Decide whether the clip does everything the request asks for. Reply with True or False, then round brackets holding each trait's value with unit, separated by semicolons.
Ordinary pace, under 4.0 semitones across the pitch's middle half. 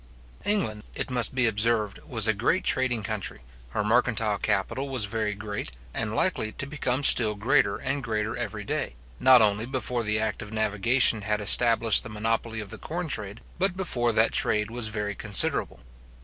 True (175 wpm; 2.8 semitones)